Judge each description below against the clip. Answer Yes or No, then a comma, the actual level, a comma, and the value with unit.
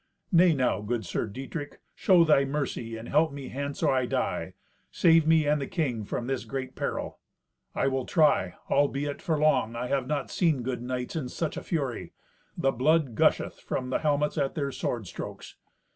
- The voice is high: No, medium, 140 Hz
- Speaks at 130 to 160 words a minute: No, average, 190 wpm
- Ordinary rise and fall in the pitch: Yes, average, 3.3 semitones